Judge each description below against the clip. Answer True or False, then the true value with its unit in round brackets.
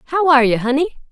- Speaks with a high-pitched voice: True (260 Hz)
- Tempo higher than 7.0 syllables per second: True (7.5 syllables/s)